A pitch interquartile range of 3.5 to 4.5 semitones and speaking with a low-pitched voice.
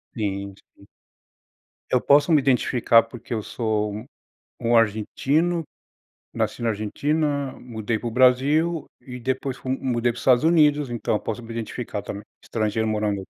Yes: average, 4.0 semitones; low, 120 Hz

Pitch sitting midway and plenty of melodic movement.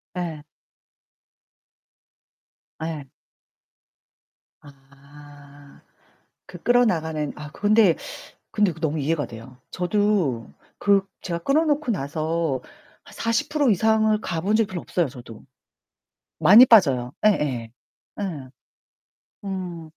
Yes: medium, 165 Hz; wide, 6.2 semitones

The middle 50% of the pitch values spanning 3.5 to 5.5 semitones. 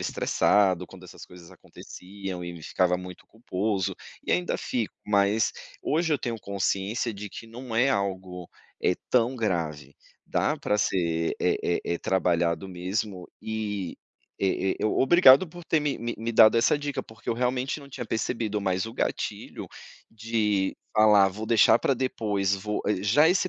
Yes: average, 3.9 semitones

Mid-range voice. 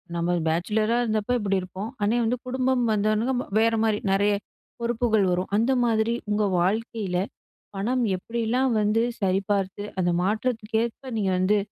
No: high, 215 Hz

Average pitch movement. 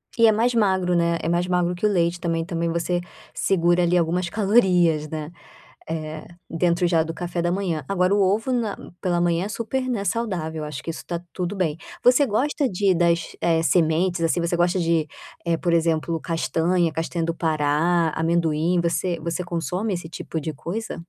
No: narrow, 2.2 semitones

